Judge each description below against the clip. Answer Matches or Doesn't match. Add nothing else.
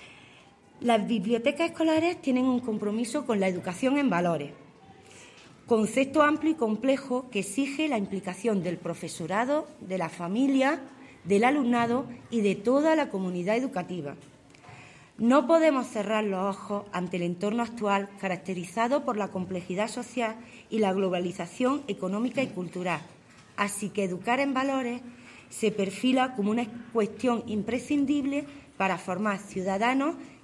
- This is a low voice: Doesn't match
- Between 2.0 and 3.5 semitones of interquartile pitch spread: Doesn't match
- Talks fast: Doesn't match